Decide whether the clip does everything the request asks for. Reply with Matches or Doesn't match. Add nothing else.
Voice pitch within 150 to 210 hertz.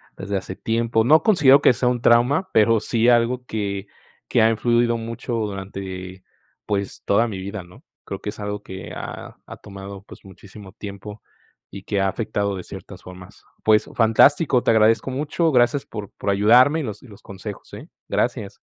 Doesn't match